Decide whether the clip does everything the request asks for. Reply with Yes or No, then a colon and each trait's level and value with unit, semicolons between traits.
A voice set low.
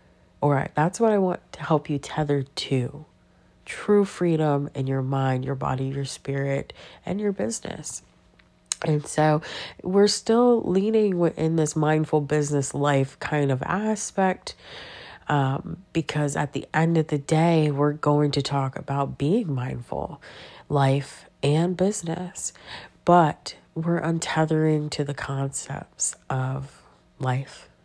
No: medium, 150 Hz